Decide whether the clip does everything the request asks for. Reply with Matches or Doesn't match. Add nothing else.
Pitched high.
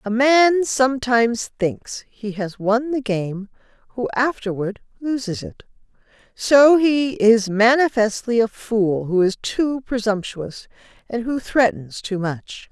Matches